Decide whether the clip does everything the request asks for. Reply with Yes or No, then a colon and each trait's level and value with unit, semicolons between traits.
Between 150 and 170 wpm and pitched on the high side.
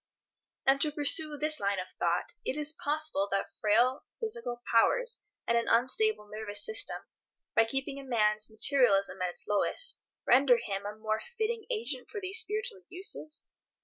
Yes: average, 160 wpm; very high, 270 Hz